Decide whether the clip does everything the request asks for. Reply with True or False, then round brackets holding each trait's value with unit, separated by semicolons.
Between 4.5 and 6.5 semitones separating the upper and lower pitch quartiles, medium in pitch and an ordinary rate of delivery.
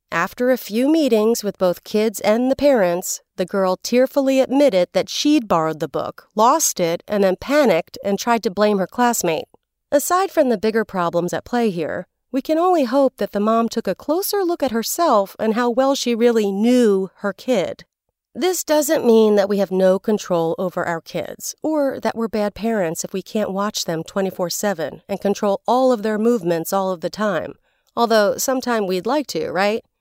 False (5.2 semitones; 220 Hz; 195 wpm)